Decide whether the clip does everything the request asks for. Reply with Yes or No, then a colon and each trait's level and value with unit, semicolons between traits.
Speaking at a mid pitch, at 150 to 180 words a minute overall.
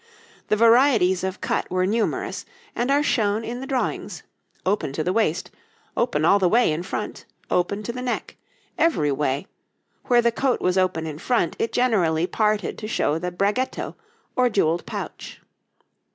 No: high, 205 Hz; average, 165 wpm